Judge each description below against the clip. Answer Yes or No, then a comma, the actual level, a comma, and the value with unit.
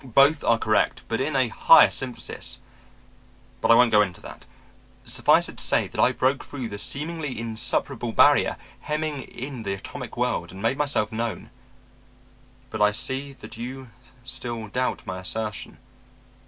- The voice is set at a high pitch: No, low, 120 Hz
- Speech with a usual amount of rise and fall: Yes, average, 3.9 semitones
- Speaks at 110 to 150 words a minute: No, average, 160 wpm